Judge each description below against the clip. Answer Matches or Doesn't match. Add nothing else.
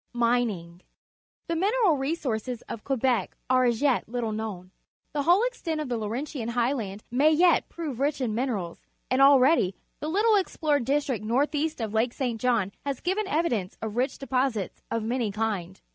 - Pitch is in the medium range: Doesn't match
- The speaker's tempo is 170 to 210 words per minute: Matches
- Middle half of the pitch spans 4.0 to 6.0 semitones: Matches